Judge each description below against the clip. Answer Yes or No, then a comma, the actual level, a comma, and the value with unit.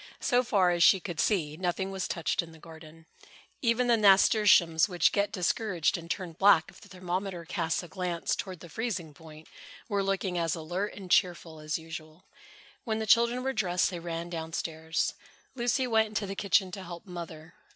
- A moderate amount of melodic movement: Yes, average, 3.5 semitones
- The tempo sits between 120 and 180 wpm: No, average, 190 wpm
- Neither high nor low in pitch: Yes, medium, 180 Hz